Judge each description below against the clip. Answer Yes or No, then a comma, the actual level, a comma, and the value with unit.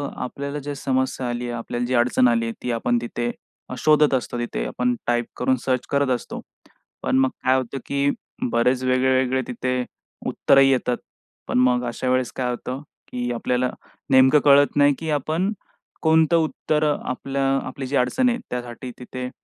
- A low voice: Yes, low, 130 Hz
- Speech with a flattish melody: Yes, narrow, 2.1 semitones